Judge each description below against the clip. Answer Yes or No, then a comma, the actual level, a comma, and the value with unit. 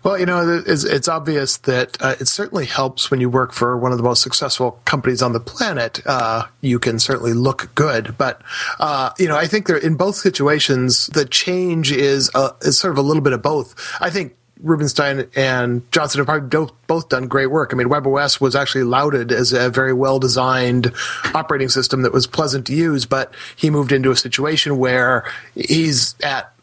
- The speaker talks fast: No, average, 195 wpm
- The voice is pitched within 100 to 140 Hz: Yes, low, 135 Hz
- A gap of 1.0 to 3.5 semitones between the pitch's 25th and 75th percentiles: Yes, average, 3.1 semitones